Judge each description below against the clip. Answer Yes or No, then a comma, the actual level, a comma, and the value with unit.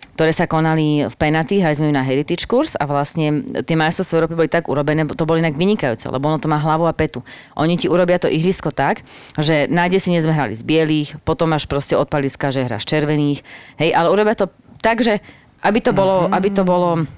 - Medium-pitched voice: Yes, medium, 155 Hz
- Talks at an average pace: No, fast, 215 wpm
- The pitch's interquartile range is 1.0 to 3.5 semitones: Yes, average, 3.0 semitones